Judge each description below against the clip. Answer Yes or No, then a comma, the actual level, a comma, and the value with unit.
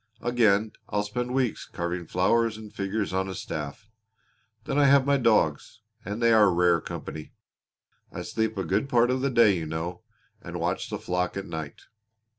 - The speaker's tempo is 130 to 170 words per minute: No, average, 180 wpm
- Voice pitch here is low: Yes, low, 105 Hz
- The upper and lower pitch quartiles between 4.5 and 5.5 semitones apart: Yes, average, 4.8 semitones